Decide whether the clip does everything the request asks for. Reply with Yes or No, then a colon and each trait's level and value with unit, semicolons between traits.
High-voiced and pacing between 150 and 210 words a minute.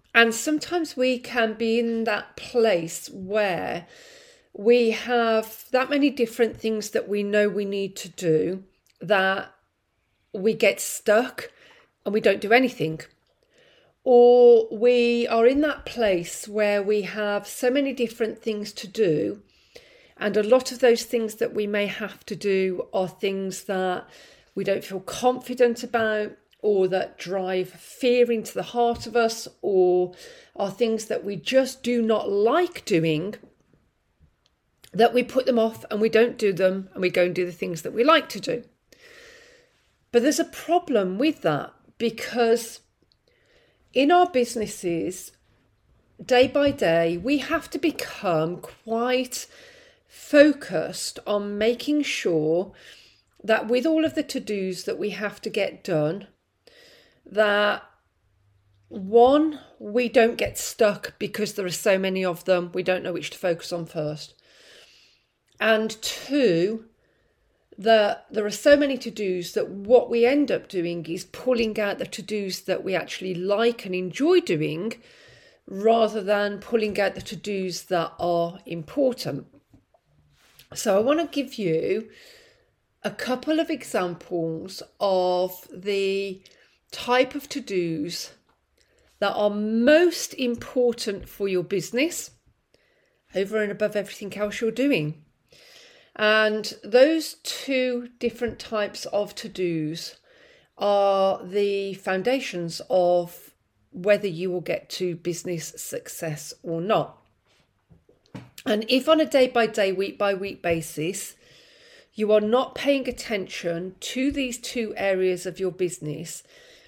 No: high, 215 Hz; average, 140 wpm